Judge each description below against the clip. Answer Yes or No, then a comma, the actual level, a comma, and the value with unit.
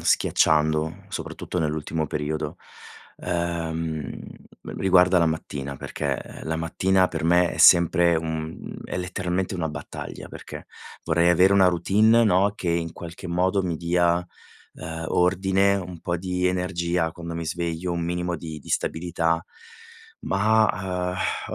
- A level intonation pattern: Yes, narrow, 2.0 semitones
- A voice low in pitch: Yes, very low, 85 Hz